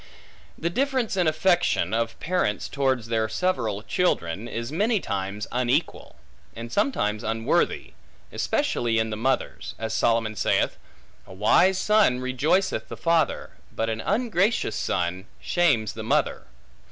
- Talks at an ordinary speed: No, slow, 130 wpm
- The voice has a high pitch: No, low, 120 Hz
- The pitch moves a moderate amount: No, wide, 8.3 semitones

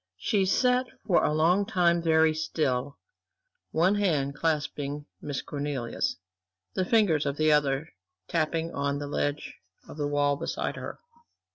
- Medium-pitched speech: Yes, medium, 155 Hz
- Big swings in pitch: No, average, 3.0 semitones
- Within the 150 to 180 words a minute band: No, average, 140 wpm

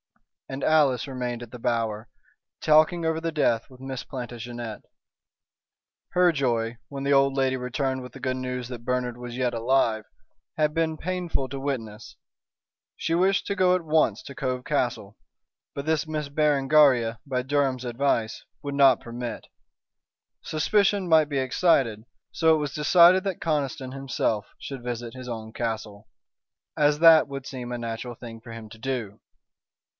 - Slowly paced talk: No, average, 160 wpm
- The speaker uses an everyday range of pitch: Yes, average, 4.1 semitones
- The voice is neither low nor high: No, low, 130 Hz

